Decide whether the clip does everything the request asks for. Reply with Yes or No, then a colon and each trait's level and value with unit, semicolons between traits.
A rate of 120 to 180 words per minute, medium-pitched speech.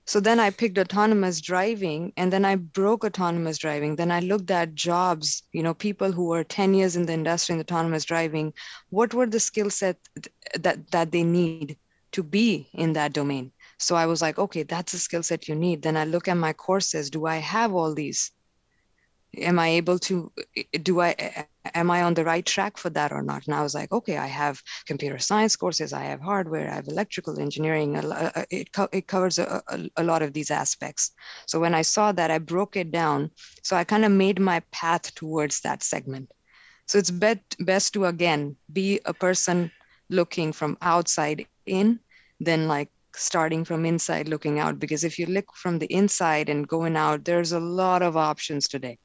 No: average, 200 wpm; medium, 170 Hz